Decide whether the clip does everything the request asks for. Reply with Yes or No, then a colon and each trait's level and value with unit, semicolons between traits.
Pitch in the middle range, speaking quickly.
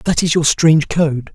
Yes: medium, 155 Hz; fast, 220 wpm